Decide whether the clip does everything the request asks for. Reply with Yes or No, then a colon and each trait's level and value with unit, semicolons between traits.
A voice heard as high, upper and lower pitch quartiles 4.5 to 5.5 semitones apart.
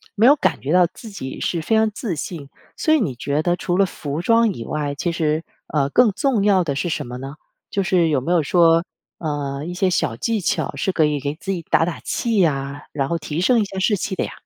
No: medium, 170 Hz; average, 5.2 semitones